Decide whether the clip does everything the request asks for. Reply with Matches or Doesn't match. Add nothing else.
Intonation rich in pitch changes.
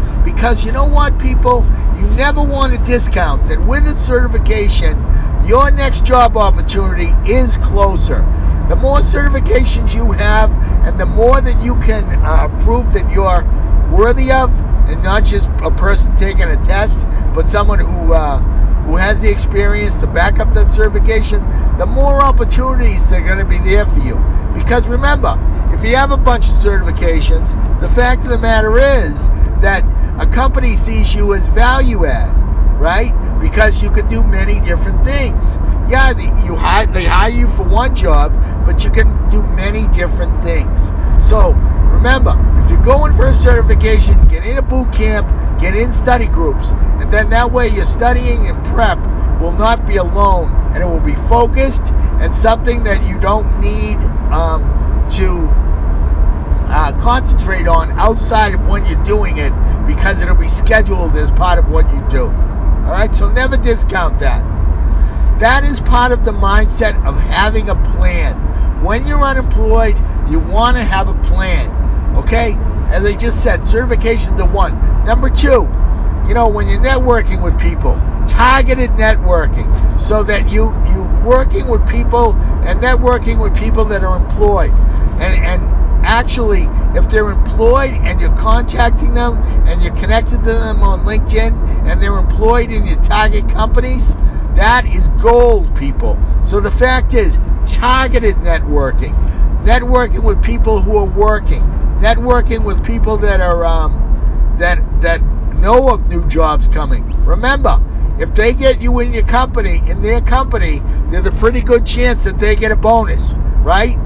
Doesn't match